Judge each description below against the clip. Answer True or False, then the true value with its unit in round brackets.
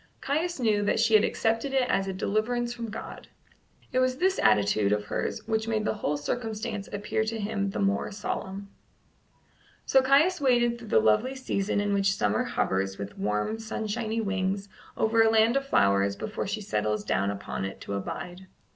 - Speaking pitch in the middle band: False (210 Hz)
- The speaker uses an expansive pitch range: True (7.9 semitones)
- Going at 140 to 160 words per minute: False (180 wpm)